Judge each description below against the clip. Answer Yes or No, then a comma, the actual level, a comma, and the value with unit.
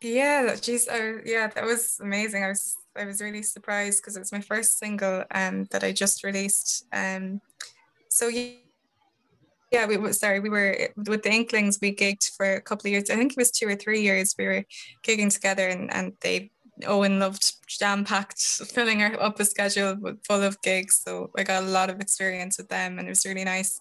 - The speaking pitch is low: No, high, 200 Hz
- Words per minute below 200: No, fast, 205 wpm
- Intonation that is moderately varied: No, narrow, 2.0 semitones